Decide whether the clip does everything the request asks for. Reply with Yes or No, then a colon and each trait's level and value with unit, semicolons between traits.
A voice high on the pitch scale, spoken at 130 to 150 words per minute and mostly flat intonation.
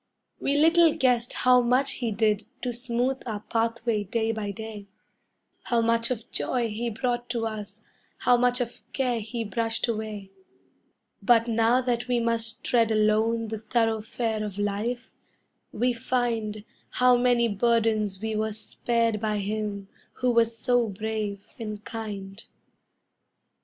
Yes: high, 225 Hz; average, 140 wpm; narrow, 2.1 semitones